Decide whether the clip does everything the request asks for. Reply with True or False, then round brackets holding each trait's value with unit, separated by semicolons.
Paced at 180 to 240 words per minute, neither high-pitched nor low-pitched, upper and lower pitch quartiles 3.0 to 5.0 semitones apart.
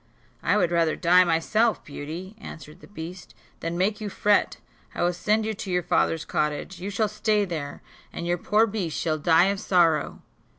True (185 wpm; 180 Hz; 4.0 semitones)